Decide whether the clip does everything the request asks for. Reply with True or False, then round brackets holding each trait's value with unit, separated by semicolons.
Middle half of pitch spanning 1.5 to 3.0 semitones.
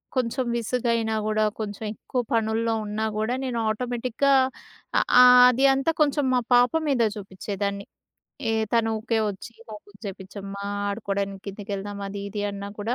False (3.4 semitones)